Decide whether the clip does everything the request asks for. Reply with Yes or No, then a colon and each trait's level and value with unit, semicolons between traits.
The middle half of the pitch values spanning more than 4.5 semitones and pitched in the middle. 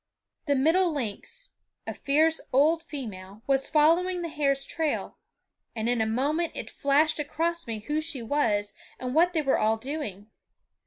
No: wide, 5.5 semitones; very high, 290 Hz